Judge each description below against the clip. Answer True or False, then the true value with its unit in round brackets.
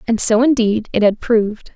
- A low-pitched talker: False (225 Hz)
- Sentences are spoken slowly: False (205 wpm)